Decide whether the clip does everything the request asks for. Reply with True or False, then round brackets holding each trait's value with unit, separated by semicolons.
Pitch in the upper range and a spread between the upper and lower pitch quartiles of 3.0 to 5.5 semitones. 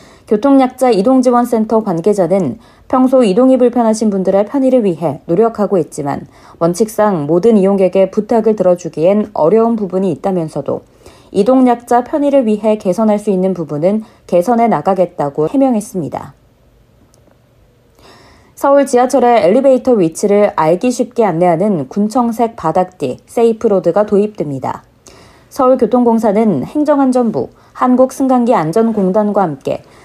True (210 Hz; 5.2 semitones)